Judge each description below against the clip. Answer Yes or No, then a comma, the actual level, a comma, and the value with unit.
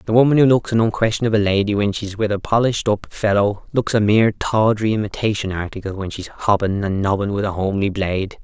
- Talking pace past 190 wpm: Yes, fast, 205 wpm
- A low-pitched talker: Yes, low, 105 Hz